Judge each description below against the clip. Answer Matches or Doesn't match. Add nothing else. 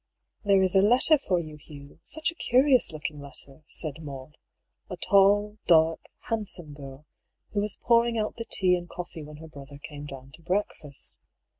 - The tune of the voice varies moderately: Doesn't match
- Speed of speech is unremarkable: Matches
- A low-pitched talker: Doesn't match